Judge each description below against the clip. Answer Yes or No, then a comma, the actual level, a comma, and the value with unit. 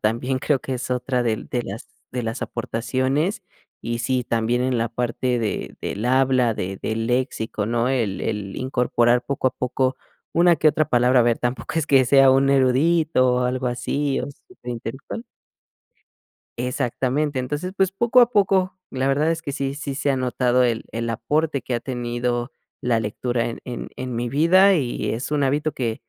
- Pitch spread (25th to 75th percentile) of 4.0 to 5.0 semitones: No, average, 2.9 semitones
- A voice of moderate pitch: No, low, 130 Hz